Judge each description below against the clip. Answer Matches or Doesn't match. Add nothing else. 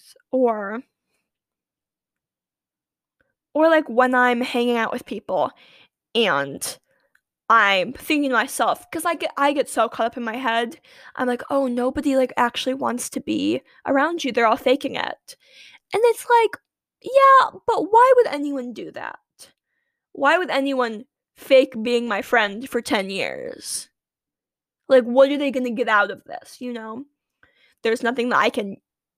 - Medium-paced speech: Matches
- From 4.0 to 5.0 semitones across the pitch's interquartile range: Doesn't match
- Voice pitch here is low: Doesn't match